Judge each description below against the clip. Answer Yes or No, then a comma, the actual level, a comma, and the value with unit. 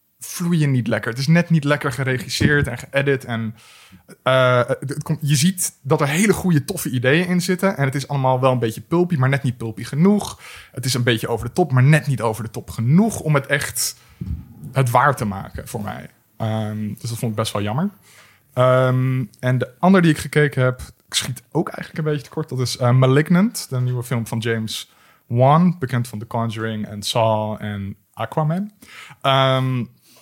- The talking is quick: Yes, fast, 205 wpm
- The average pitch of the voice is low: Yes, low, 130 Hz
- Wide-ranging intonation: No, average, 4.5 semitones